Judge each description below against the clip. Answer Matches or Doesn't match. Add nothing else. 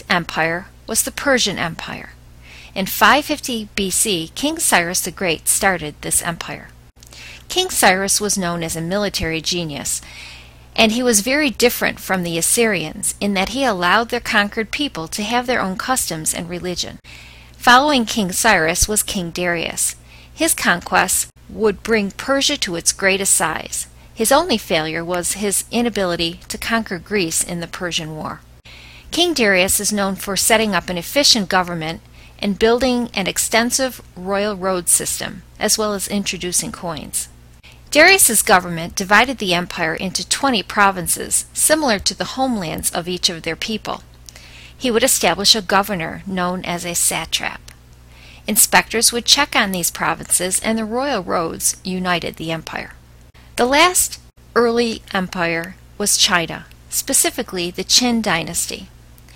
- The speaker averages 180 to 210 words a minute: Doesn't match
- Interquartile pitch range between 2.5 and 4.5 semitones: Doesn't match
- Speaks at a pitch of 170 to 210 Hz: Matches